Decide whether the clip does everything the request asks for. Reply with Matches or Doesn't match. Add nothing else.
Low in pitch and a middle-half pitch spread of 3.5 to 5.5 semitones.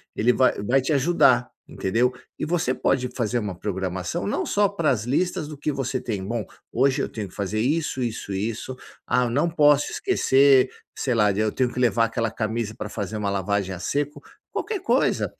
Matches